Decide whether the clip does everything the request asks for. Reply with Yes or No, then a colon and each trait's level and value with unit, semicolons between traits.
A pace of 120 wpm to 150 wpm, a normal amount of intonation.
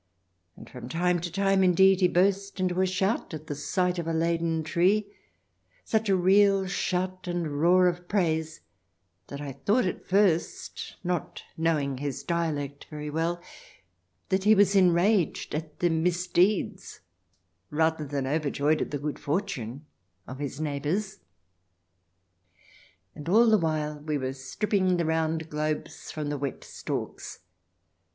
Yes: average, 145 wpm; average, 3.9 semitones